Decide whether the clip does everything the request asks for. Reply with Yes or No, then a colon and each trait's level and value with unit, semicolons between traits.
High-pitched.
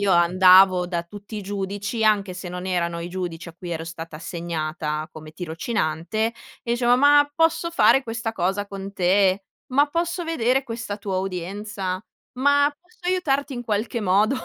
Yes: high, 200 Hz